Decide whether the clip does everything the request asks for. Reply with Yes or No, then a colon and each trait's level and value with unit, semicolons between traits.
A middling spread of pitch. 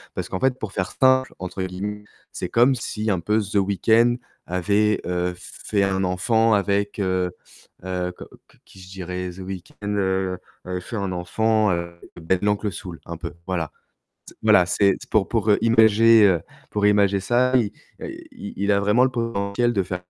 Yes: average, 3.0 semitones